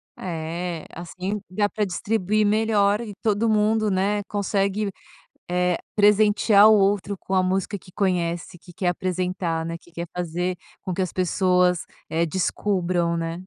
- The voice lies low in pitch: No, medium, 185 Hz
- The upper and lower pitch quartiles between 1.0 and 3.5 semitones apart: Yes, narrow, 2.6 semitones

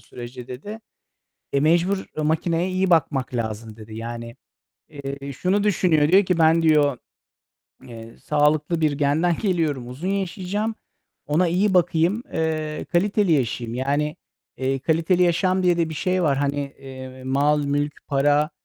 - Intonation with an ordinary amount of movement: Yes, average, 4.5 semitones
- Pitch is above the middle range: No, medium, 150 Hz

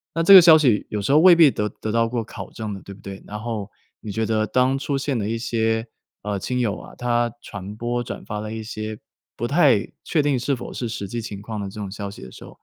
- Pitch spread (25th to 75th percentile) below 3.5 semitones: Yes, average, 3.1 semitones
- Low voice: Yes, low, 115 Hz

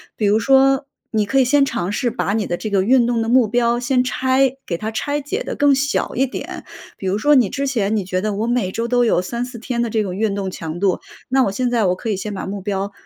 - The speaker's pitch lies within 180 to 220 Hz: No, high, 230 Hz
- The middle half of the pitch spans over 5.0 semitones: No, average, 4.4 semitones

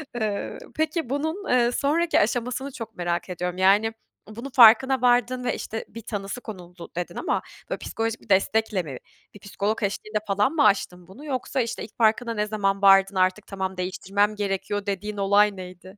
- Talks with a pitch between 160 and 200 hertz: No, high, 210 Hz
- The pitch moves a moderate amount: Yes, average, 3.7 semitones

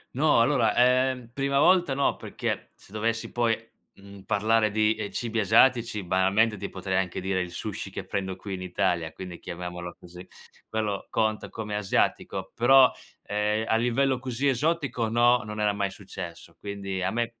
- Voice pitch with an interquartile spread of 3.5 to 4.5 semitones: Yes, average, 4.0 semitones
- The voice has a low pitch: Yes, low, 110 Hz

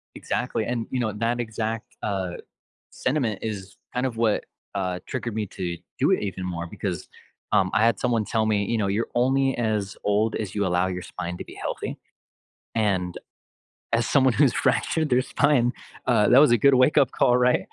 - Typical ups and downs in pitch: Yes, average, 3.9 semitones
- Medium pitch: No, low, 110 Hz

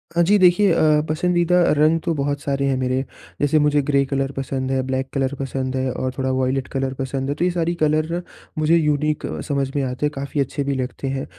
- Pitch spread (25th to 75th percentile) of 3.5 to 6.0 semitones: No, average, 2.7 semitones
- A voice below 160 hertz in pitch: Yes, medium, 140 Hz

